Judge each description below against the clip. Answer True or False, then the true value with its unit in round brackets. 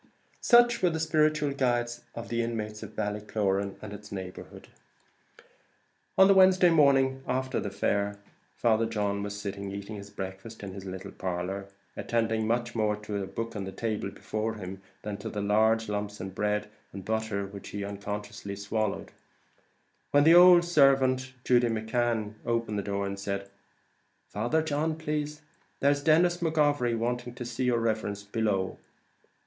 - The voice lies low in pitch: True (110 Hz)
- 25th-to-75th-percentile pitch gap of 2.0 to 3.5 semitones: False (4.5 semitones)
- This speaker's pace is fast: False (165 wpm)